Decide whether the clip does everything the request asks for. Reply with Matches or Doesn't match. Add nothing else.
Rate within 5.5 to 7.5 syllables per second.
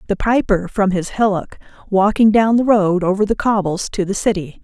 Doesn't match